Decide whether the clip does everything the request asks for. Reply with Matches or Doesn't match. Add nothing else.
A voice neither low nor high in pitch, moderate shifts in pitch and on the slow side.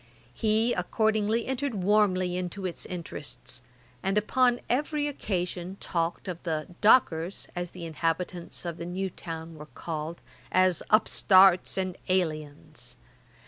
Matches